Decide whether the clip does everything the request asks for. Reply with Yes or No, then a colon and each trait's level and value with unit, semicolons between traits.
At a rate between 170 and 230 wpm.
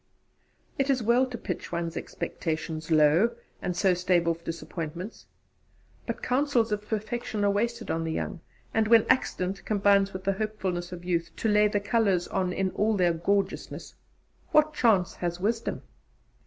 No: average, 160 wpm